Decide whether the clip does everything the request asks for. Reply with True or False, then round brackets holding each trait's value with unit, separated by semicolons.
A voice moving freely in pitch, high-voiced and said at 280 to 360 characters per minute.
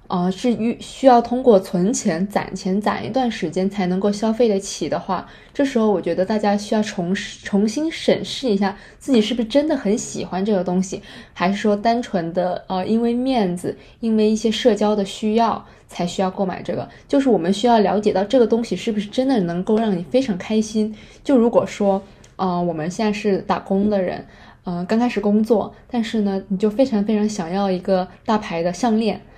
False (3.2 semitones; 210 Hz; 305 characters per minute)